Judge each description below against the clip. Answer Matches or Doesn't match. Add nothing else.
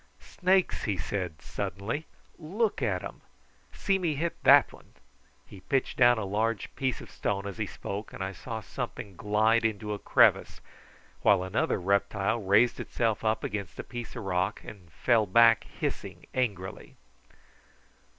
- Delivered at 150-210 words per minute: Matches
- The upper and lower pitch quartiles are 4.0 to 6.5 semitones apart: Doesn't match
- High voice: Doesn't match